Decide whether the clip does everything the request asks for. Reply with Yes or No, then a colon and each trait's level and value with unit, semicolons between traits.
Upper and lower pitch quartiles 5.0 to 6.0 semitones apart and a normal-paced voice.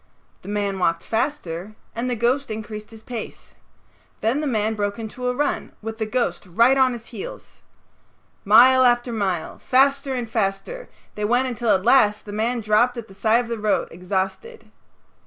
No: average, 3.2 semitones; average, 175 wpm